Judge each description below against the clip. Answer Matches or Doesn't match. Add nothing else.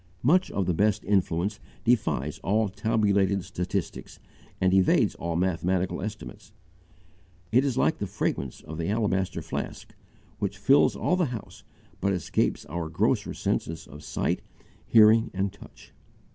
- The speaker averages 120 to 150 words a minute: Matches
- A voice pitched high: Doesn't match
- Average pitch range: Matches